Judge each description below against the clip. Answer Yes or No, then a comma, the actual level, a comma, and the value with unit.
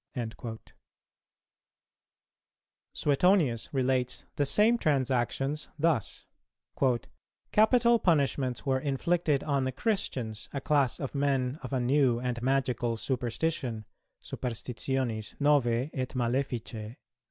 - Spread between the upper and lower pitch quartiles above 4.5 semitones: No, average, 3.2 semitones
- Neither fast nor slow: No, slow, 95 wpm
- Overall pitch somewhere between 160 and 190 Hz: No, low, 135 Hz